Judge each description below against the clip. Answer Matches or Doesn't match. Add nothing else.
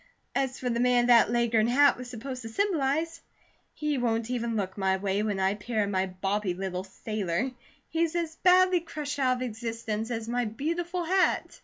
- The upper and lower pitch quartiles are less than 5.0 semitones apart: Doesn't match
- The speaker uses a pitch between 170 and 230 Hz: Doesn't match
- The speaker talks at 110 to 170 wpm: Doesn't match